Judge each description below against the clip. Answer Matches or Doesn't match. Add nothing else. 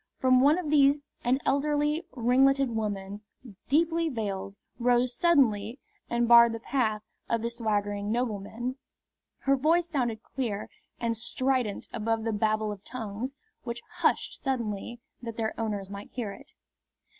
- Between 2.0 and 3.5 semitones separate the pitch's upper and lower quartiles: Doesn't match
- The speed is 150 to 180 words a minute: Doesn't match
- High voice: Matches